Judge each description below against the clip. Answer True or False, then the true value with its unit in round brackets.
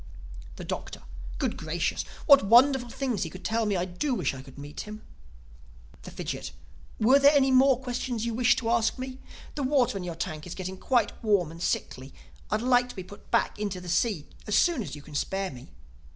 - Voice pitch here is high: True (215 Hz)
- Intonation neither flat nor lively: False (6.0 semitones)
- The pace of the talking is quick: True (210 wpm)